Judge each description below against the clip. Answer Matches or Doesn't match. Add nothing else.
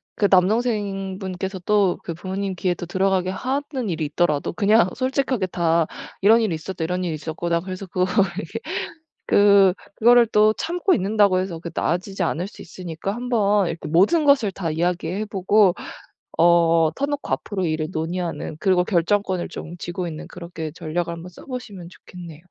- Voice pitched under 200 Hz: Matches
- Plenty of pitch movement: Doesn't match